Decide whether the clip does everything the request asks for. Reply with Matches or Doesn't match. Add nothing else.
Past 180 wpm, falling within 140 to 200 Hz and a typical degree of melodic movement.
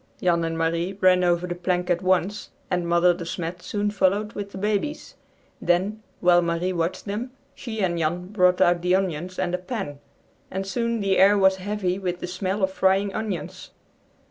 Doesn't match